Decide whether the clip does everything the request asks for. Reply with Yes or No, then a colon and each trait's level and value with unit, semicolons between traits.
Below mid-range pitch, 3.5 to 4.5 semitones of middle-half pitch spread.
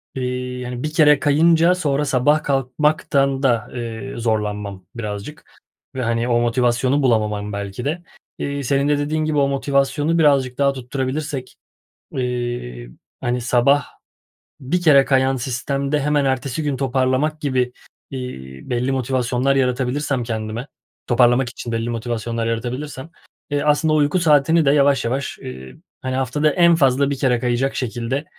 No: low, 130 Hz; average, 3.0 semitones